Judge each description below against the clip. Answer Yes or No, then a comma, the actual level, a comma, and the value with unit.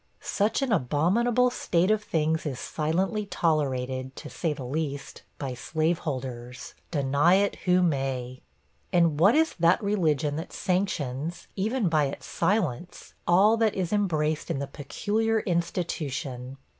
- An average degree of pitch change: No, wide, 5.8 semitones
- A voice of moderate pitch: Yes, medium, 165 Hz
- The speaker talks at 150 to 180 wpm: No, slow, 135 wpm